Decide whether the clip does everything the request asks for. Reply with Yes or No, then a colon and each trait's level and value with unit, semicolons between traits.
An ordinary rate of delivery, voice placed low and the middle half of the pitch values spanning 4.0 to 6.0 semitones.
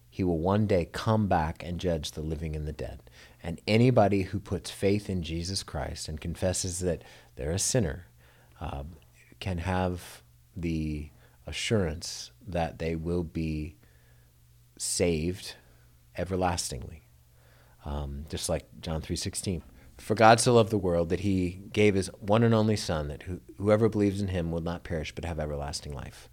Yes: average, 160 wpm; very low, 85 Hz; average, 5.2 semitones